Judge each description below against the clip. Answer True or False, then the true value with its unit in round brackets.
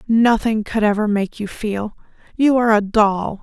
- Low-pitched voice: False (215 Hz)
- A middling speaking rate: True (175 wpm)